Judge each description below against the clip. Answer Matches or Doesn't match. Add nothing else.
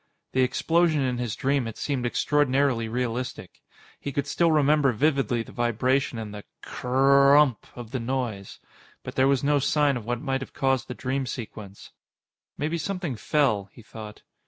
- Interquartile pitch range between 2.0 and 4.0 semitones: Matches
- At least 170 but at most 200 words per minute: Matches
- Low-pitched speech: Matches